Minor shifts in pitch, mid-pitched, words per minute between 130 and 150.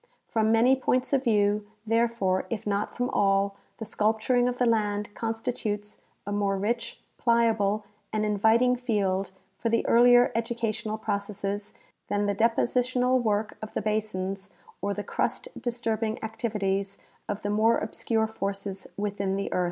No: narrow, 2.3 semitones; high, 215 Hz; average, 145 wpm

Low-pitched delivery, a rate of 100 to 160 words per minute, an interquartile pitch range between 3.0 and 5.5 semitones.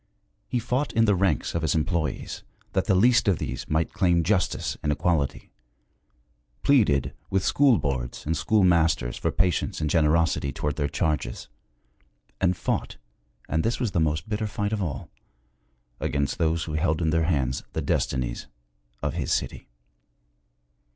Yes: very low, 80 Hz; average, 155 wpm; average, 4.7 semitones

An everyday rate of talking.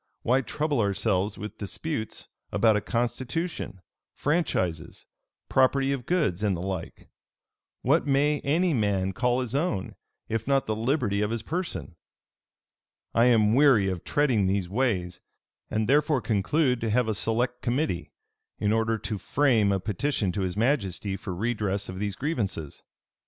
Yes: average, 150 wpm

